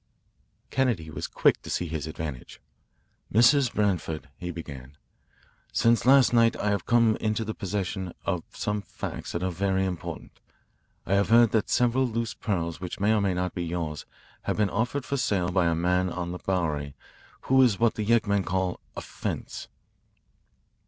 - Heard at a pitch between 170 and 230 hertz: No, very low, 95 Hz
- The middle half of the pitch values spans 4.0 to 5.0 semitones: Yes, average, 4.6 semitones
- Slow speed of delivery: No, average, 170 wpm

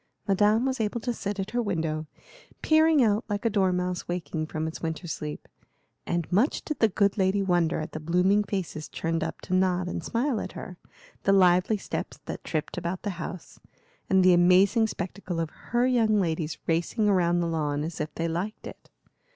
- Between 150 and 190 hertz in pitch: Yes, medium, 185 Hz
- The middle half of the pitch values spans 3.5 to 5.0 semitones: Yes, average, 3.8 semitones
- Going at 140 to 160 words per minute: No, average, 190 wpm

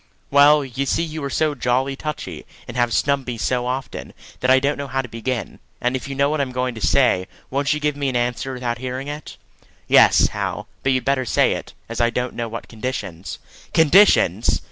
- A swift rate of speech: Yes, fast, 220 wpm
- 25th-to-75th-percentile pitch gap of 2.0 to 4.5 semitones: Yes, narrow, 2.4 semitones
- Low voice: Yes, low, 130 Hz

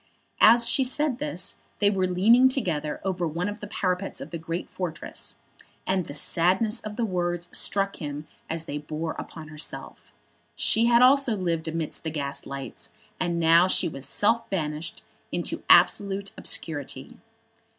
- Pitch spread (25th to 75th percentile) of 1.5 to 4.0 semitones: No, average, 4.6 semitones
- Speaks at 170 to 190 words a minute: No, average, 155 wpm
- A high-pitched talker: No, medium, 180 Hz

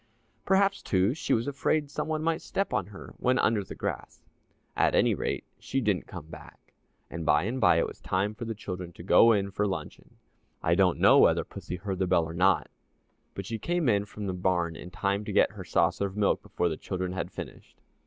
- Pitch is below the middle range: Yes, low, 100 Hz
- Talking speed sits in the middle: No, fast, 225 wpm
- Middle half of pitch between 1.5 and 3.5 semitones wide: No, average, 4.1 semitones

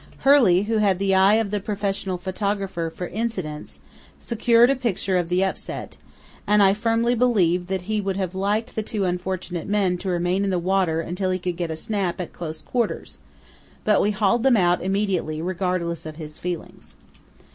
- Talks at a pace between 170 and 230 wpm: Yes, average, 185 wpm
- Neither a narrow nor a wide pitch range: Yes, average, 3.0 semitones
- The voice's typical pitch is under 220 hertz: Yes, high, 190 Hz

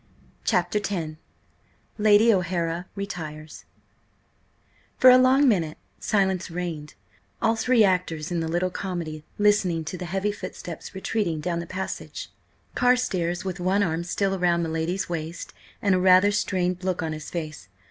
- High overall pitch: No, medium, 180 Hz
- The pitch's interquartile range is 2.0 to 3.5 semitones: Yes, average, 3.2 semitones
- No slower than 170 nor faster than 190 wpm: No, average, 145 wpm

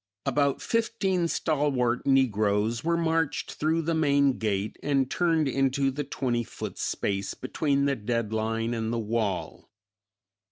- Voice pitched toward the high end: No, low, 135 Hz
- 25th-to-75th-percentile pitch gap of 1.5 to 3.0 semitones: No, average, 4.9 semitones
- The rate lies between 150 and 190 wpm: No, slow, 135 wpm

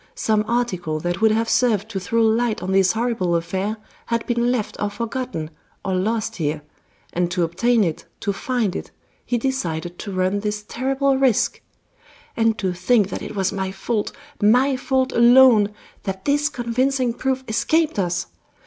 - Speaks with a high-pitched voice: Yes, high, 220 Hz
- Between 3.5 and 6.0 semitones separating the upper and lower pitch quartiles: Yes, average, 4.5 semitones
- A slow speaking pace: No, average, 165 wpm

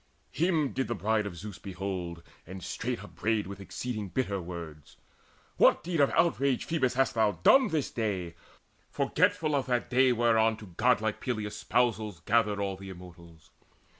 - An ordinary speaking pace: Yes, average, 160 wpm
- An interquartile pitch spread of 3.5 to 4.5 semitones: No, average, 5.0 semitones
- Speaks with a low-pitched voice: Yes, low, 110 Hz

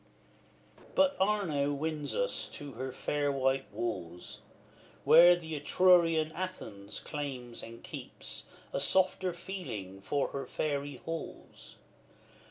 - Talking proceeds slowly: Yes, slow, 115 wpm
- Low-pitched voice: No, medium, 145 Hz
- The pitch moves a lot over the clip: No, average, 4.9 semitones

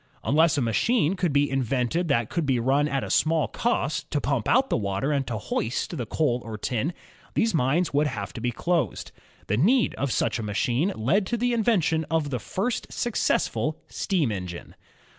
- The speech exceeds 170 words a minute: Yes, average, 200 wpm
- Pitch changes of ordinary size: No, wide, 6.5 semitones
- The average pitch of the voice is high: No, medium, 145 Hz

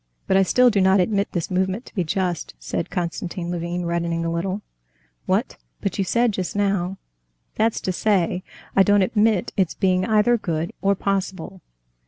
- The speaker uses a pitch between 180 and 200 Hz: Yes, high, 190 Hz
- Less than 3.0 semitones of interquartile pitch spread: Yes, narrow, 2.6 semitones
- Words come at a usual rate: Yes, average, 175 wpm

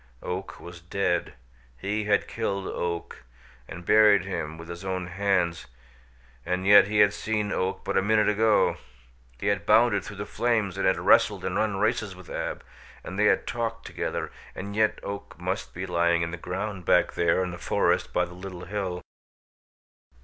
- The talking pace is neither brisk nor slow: Yes, average, 180 wpm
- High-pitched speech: No, very low, 95 Hz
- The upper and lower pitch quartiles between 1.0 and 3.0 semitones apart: Yes, narrow, 2.6 semitones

